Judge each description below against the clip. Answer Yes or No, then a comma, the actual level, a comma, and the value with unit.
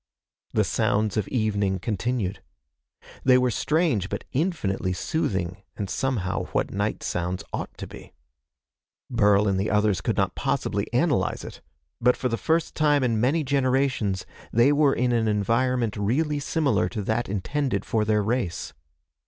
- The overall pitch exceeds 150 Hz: No, low, 115 Hz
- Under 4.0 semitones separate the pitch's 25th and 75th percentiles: No, average, 4.8 semitones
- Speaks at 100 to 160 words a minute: Yes, average, 155 wpm